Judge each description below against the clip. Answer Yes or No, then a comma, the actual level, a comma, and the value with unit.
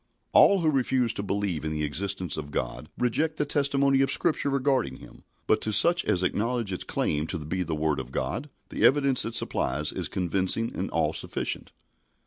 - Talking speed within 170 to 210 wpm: Yes, average, 190 wpm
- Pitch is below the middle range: Yes, low, 105 Hz